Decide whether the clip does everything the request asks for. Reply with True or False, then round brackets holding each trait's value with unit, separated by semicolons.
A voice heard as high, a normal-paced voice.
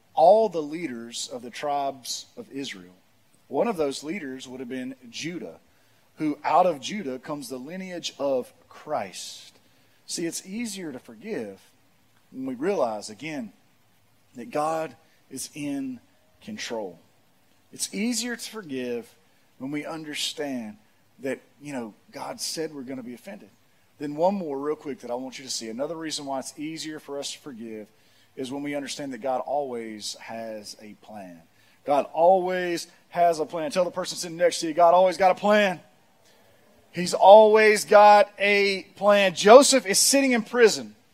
False (155 Hz; 165 wpm)